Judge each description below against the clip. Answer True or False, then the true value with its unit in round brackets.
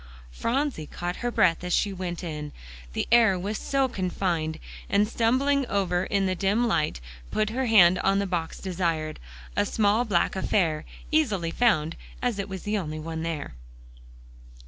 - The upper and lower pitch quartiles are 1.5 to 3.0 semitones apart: False (4.8 semitones)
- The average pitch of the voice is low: False (190 Hz)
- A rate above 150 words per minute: True (165 wpm)